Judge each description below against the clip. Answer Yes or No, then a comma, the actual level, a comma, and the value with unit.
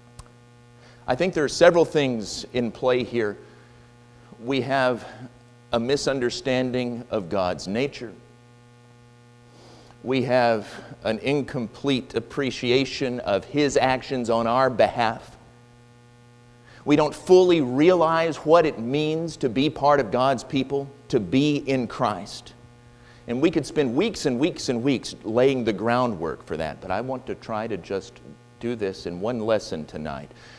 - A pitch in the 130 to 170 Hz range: No, low, 120 Hz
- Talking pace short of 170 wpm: Yes, average, 140 wpm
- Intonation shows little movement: Yes, narrow, 2.1 semitones